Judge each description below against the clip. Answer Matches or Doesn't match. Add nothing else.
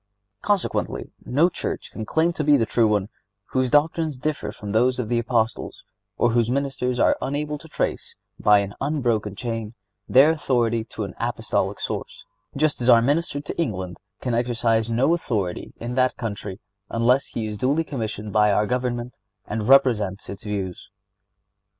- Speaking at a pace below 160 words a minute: Doesn't match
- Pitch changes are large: Doesn't match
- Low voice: Matches